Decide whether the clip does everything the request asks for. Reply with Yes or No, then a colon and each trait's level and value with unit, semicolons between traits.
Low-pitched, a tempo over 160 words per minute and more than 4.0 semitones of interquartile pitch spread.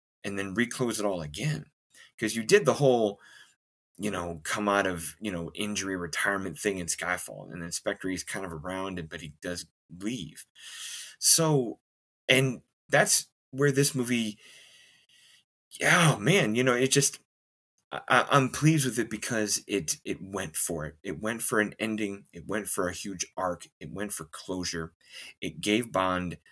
Yes: low, 105 Hz; average, 175 wpm; wide, 5.6 semitones